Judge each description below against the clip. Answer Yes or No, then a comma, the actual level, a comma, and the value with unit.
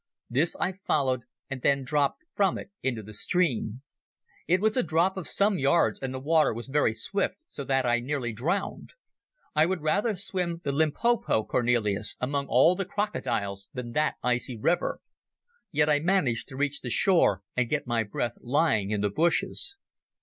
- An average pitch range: No, wide, 6.3 semitones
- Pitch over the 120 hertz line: Yes, medium, 140 Hz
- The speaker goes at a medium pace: Yes, average, 175 wpm